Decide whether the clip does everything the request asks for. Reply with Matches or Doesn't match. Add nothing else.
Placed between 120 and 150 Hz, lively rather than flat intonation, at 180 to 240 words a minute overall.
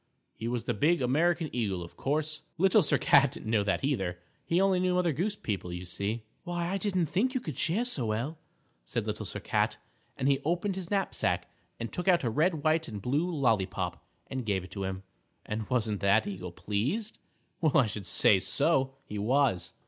Matches